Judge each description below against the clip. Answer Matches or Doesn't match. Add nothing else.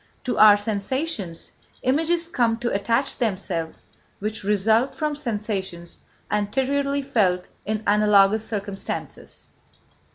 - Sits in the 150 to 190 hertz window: Doesn't match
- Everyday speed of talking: Doesn't match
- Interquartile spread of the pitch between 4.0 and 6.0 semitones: Matches